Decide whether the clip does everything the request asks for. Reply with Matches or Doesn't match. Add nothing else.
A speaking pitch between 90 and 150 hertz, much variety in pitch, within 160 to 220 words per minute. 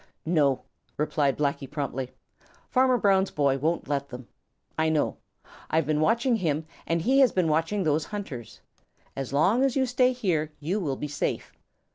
Doesn't match